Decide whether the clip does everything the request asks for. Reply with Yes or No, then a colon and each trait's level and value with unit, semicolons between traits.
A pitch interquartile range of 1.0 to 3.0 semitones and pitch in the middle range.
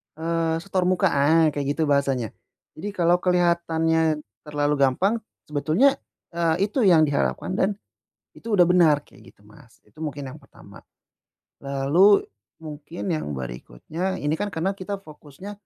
No: average, 4.0 semitones; medium, 160 Hz